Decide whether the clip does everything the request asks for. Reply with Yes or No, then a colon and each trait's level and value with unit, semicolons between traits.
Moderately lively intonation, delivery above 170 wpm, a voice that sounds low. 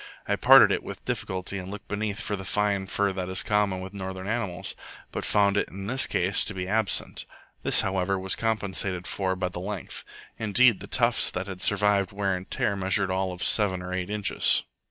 No: narrow, 1.8 semitones; fast, 205 wpm; very low, 95 Hz